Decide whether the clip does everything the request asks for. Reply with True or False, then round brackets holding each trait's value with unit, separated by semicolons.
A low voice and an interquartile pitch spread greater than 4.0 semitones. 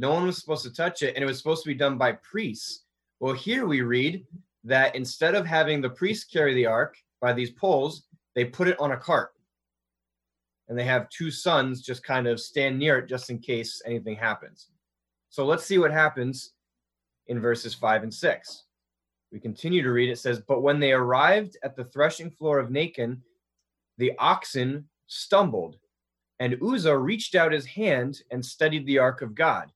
True (130 Hz; 4.8 semitones)